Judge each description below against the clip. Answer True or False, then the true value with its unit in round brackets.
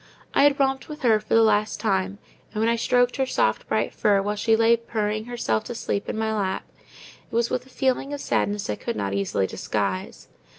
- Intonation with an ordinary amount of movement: True (3.4 semitones)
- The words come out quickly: True (220 wpm)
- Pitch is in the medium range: False (220 Hz)